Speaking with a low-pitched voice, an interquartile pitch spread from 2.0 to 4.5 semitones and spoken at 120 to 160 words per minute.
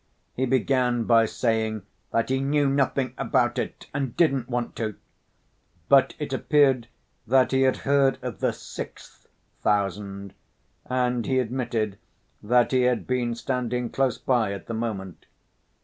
Yes: low, 125 Hz; average, 2.8 semitones; average, 145 wpm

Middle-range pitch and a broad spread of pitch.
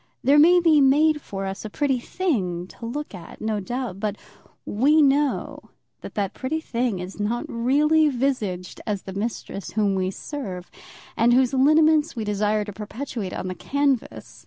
No: high, 240 Hz; wide, 6.2 semitones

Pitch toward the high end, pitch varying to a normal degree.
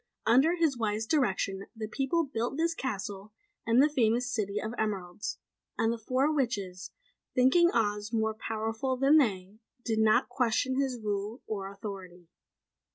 Yes: high, 225 Hz; average, 4.1 semitones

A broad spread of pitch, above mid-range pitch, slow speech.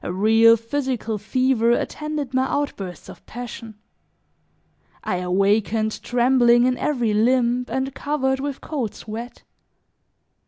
No: average, 3.3 semitones; high, 240 Hz; slow, 115 wpm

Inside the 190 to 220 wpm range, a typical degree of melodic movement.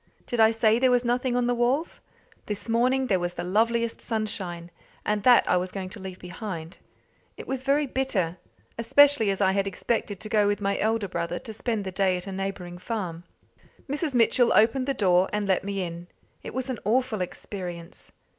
Yes: average, 200 wpm; average, 4.5 semitones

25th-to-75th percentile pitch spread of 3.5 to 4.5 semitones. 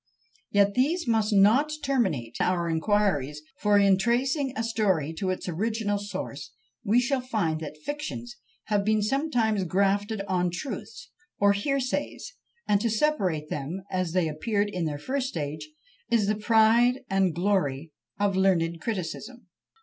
No: average, 5.0 semitones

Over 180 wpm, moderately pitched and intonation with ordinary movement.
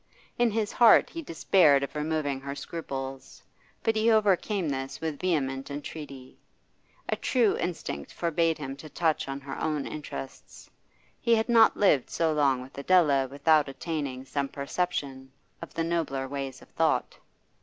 No: average, 155 wpm; medium, 150 Hz; average, 4.1 semitones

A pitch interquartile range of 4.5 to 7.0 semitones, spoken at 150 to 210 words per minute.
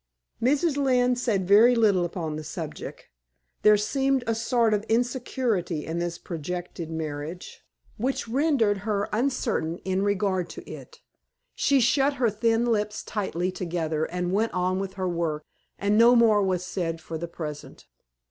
Yes: average, 5.2 semitones; average, 155 wpm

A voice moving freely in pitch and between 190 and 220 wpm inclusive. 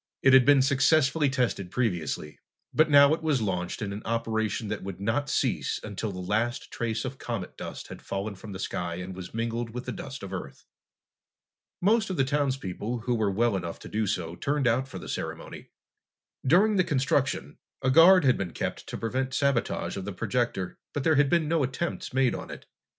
Yes: wide, 5.8 semitones; fast, 205 wpm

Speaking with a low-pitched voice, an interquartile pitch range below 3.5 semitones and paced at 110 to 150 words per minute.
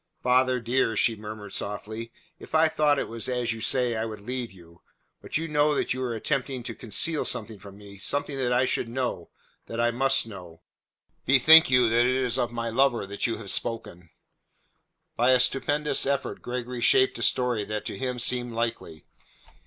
No: low, 120 Hz; average, 2.8 semitones; average, 195 wpm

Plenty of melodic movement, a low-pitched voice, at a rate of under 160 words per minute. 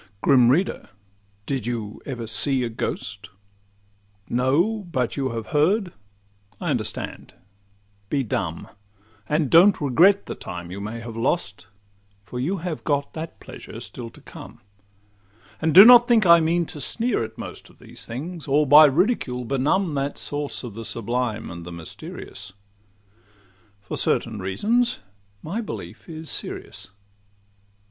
Yes: wide, 7.2 semitones; low, 130 Hz; average, 140 wpm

